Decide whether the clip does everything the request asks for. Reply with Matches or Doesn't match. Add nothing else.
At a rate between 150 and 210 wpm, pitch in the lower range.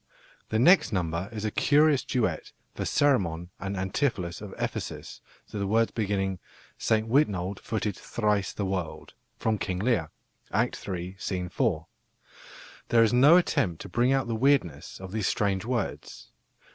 Matches